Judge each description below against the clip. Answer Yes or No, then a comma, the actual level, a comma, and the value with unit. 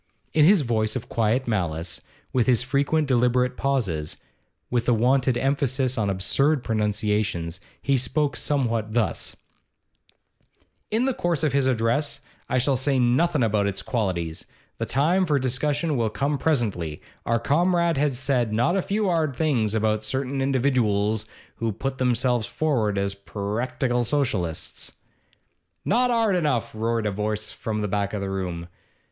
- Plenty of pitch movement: No, average, 4.7 semitones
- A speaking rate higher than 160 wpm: No, average, 150 wpm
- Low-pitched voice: Yes, low, 125 Hz